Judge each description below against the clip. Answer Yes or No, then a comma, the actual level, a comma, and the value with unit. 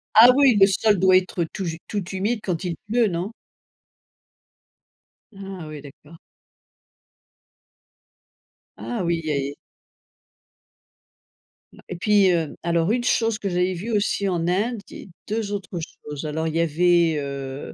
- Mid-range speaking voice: Yes, medium, 180 Hz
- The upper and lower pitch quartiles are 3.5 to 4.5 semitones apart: Yes, average, 4.0 semitones